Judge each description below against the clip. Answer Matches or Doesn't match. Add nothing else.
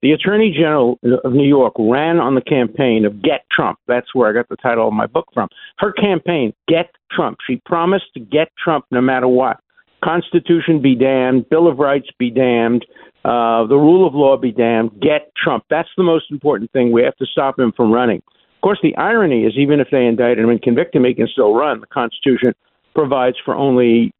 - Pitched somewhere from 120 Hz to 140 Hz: Matches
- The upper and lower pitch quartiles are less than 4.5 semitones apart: Doesn't match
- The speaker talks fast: Matches